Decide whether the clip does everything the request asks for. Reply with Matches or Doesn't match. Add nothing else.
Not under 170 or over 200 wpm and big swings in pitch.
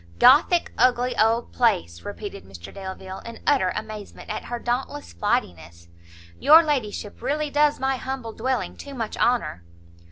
Doesn't match